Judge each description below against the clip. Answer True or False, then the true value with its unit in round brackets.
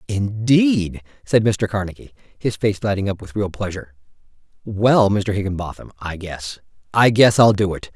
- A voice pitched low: True (105 Hz)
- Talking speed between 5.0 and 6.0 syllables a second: True (5.1 syllables/s)